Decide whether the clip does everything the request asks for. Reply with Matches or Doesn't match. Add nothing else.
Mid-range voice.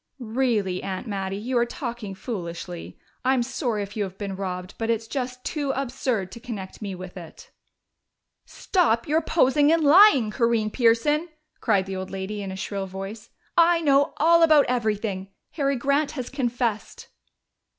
Doesn't match